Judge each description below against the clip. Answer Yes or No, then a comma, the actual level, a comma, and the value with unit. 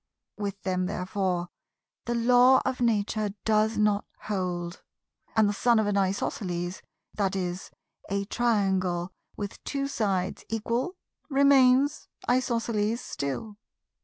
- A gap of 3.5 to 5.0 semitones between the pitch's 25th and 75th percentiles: Yes, average, 4.0 semitones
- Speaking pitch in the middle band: No, high, 210 Hz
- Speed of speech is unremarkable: No, slow, 110 wpm